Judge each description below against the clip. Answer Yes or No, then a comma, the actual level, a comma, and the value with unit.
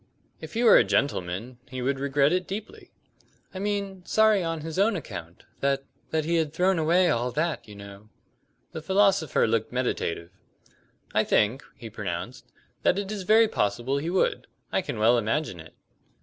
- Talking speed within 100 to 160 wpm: No, average, 175 wpm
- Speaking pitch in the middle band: Yes, medium, 145 Hz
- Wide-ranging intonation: Yes, wide, 8.6 semitones